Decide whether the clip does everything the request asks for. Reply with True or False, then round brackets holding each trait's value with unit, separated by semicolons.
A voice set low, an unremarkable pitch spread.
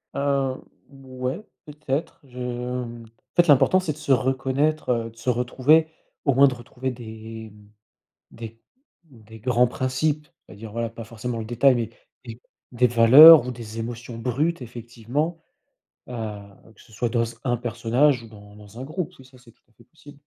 True (125 Hz; 3.1 semitones)